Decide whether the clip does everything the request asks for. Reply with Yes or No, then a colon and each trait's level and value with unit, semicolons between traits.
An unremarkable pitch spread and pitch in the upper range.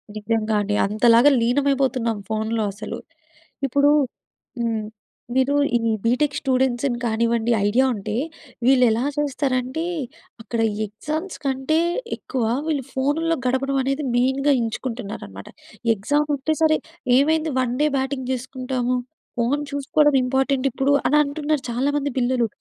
Yes: average, 3.3 semitones; very high, 260 Hz